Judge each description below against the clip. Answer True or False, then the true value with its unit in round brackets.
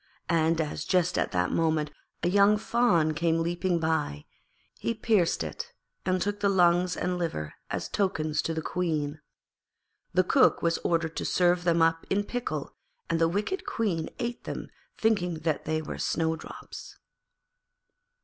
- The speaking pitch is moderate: True (170 Hz)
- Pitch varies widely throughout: False (3.5 semitones)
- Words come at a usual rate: True (155 wpm)